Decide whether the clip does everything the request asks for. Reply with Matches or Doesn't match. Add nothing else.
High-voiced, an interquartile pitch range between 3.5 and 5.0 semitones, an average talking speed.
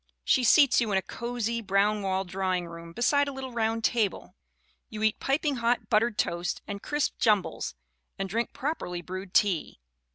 Matches